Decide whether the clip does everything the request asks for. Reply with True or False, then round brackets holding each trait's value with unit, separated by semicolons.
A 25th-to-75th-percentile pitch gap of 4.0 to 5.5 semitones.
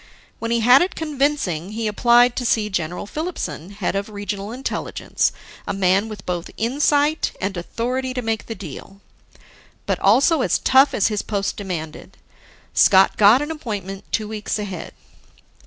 True (4.5 semitones)